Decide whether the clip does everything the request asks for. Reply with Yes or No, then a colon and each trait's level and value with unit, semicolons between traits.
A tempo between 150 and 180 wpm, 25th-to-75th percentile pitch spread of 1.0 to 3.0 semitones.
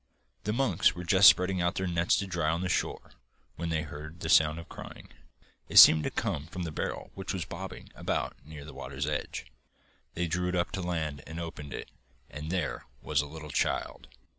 No: fast, 205 wpm; narrow, 2.6 semitones